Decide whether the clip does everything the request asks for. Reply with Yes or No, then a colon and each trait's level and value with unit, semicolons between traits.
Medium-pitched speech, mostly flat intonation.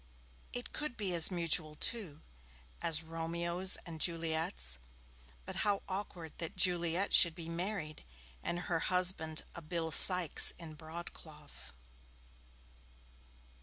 Yes: medium, 170 Hz; narrow, 2.3 semitones